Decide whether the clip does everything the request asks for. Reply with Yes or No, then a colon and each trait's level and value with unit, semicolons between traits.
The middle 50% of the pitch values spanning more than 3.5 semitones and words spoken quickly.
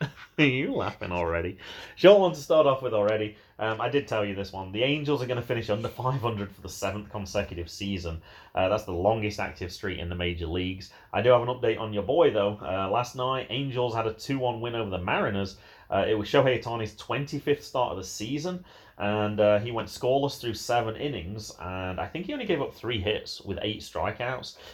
Yes: average, 4.3 semitones; fast, 220 wpm